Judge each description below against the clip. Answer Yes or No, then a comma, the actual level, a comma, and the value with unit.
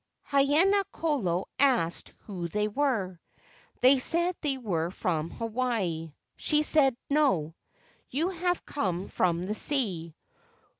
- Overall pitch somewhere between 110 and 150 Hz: No, high, 235 Hz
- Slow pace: Yes, slow, 115 wpm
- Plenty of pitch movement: Yes, wide, 8.6 semitones